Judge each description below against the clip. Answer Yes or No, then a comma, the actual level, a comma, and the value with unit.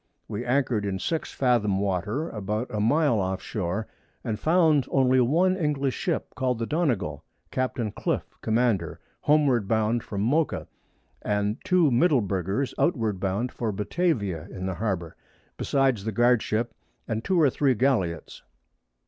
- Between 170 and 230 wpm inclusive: No, average, 145 wpm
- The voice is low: Yes, low, 115 Hz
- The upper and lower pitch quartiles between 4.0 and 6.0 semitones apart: Yes, average, 5.2 semitones